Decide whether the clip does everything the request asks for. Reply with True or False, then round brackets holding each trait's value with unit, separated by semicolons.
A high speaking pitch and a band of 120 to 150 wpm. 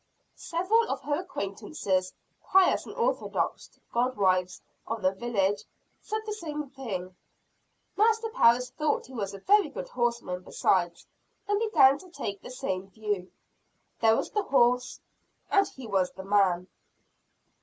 True (240 Hz; 140 wpm)